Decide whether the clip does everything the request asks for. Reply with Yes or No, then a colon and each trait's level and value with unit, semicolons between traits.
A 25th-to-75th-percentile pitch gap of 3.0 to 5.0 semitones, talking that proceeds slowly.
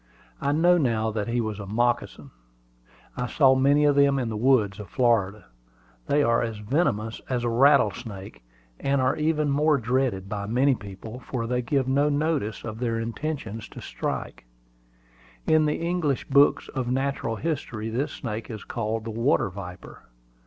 No: average, 4.3 semitones; average, 165 wpm